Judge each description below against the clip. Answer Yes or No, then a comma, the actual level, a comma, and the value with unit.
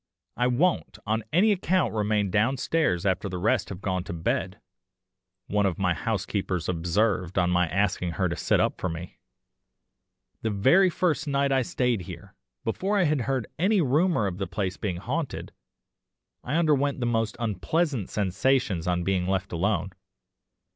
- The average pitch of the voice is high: No, low, 105 Hz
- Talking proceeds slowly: No, average, 160 wpm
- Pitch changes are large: Yes, wide, 6.7 semitones